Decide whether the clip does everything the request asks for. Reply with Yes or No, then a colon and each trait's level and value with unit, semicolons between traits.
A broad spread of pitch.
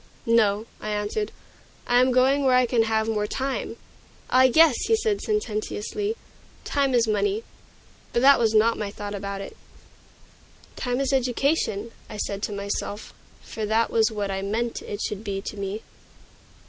No: average, 4.0 semitones